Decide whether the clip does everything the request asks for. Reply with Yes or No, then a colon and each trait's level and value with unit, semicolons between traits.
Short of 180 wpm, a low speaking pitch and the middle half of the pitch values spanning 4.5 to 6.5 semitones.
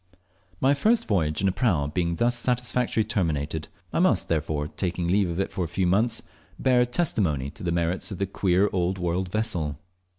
No: average, 185 wpm; very low, 95 Hz; average, 5.0 semitones